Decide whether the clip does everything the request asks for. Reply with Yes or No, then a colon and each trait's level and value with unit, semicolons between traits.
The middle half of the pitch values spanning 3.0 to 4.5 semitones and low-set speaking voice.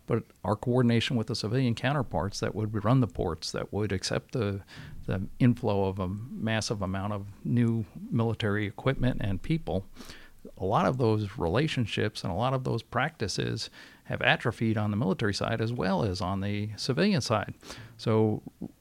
Yes: average, 3.5 semitones; low, 110 Hz